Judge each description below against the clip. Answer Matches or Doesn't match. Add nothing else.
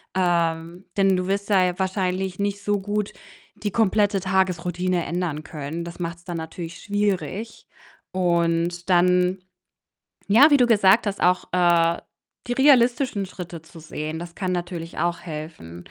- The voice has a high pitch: Doesn't match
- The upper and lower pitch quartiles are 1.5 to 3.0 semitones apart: Matches